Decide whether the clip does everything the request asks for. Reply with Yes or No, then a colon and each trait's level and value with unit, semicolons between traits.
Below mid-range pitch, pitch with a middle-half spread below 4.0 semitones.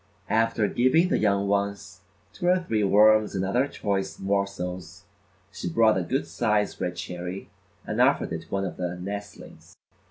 Yes: low, 100 Hz; average, 2.8 semitones